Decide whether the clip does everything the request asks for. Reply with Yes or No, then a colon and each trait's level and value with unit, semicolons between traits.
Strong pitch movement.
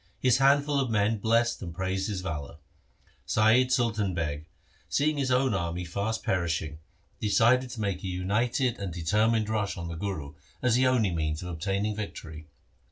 Yes: wide, 5.7 semitones